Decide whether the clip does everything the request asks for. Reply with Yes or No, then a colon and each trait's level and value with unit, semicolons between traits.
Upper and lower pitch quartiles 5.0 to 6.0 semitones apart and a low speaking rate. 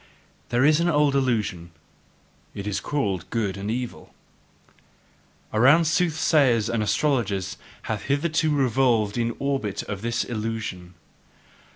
Yes: average, 5.3 semitones; slow, 115 wpm